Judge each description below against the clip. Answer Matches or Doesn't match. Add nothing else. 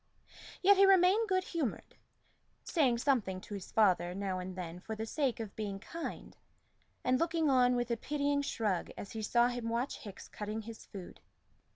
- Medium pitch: Doesn't match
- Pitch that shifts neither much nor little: Doesn't match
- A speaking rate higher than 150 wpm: Matches